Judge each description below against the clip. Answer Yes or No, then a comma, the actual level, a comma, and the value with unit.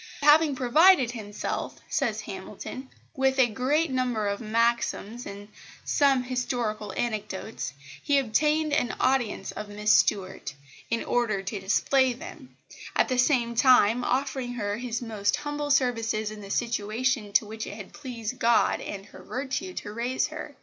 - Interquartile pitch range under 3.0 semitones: No, average, 3.7 semitones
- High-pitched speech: Yes, high, 240 Hz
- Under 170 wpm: Yes, average, 150 wpm